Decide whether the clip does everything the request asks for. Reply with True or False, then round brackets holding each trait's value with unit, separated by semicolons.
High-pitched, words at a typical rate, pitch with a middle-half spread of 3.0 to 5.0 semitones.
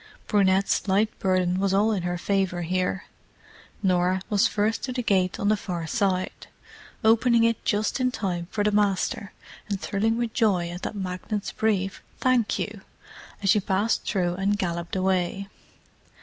False (195 Hz; 160 wpm; 2.5 semitones)